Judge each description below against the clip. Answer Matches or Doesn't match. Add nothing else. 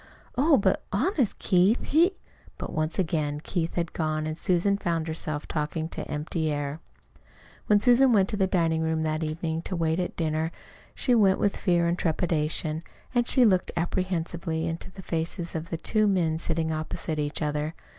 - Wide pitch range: Doesn't match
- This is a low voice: Doesn't match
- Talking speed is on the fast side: Doesn't match